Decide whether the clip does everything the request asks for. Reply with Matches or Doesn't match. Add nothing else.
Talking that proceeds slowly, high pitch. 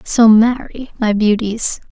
Matches